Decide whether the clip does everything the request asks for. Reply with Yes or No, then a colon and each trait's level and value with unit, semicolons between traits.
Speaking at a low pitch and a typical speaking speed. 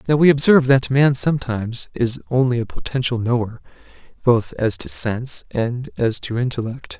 Yes: low, 125 Hz; average, 165 wpm